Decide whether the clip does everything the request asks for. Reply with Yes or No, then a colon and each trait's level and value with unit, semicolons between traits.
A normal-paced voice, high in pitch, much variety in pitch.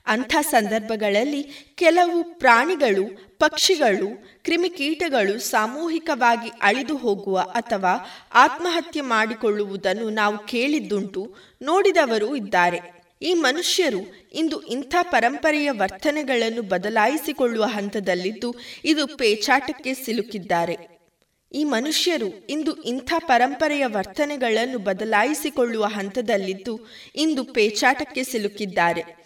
Yes: average, 80 wpm; high, 240 Hz; wide, 6.5 semitones